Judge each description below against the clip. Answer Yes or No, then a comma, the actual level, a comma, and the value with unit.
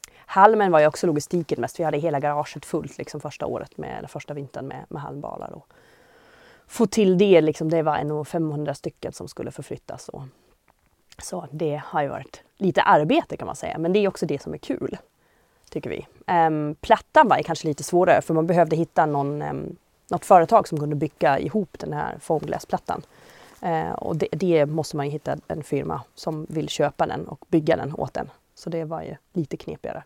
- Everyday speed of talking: No, fast, 200 wpm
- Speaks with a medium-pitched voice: Yes, medium, 160 Hz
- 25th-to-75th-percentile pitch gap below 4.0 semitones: Yes, average, 3.2 semitones